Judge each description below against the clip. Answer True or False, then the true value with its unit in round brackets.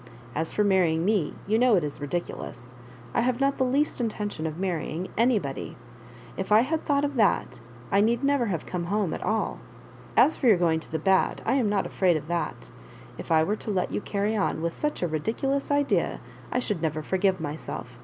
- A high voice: True (195 Hz)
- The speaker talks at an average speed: False (215 wpm)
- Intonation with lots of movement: True (6.4 semitones)